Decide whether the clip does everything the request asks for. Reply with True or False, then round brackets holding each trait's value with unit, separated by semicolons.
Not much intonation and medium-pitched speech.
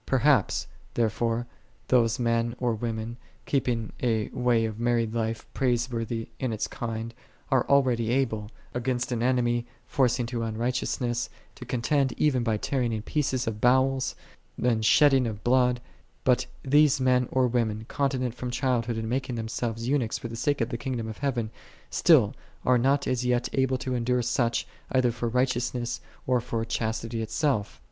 False (2.0 semitones; 120 Hz)